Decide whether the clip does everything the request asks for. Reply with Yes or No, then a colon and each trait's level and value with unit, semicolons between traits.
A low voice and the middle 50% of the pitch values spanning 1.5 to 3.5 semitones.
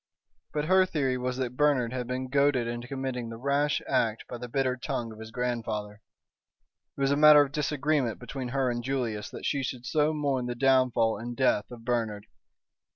Yes: low, 125 Hz; average, 2.7 semitones